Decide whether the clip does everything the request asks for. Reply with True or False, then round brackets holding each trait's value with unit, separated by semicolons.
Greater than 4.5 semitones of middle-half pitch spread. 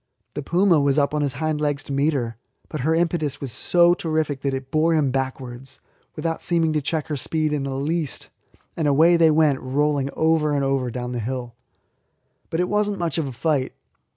False (3.0 semitones)